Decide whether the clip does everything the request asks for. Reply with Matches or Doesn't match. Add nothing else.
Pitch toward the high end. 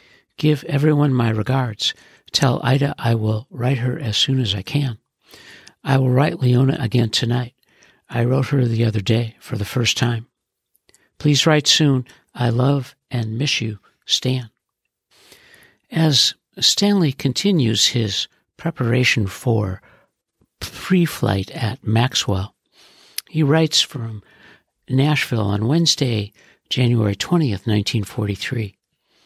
Doesn't match